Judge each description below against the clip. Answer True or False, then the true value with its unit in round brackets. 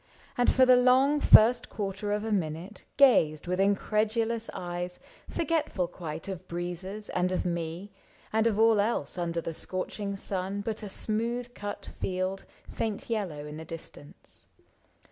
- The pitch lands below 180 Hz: False (200 Hz)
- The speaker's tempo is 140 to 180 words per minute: True (150 wpm)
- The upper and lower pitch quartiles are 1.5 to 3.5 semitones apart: False (4.0 semitones)